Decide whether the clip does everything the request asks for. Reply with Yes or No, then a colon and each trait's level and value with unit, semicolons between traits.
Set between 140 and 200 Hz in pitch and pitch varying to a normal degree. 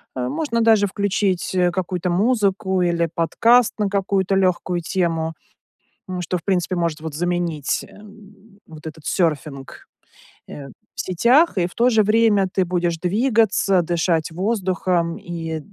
Yes: medium, 185 Hz; average, 3.3 semitones